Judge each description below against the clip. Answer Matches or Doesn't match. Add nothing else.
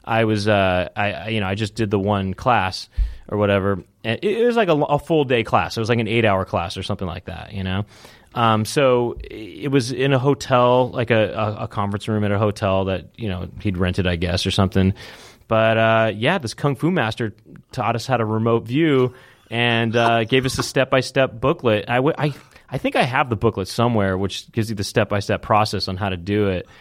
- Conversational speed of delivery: Doesn't match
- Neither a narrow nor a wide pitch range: Matches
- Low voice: Matches